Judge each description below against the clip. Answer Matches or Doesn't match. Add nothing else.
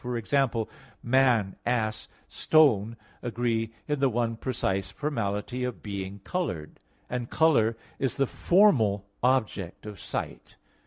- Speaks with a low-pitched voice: Matches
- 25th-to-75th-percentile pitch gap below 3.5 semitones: Doesn't match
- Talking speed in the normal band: Doesn't match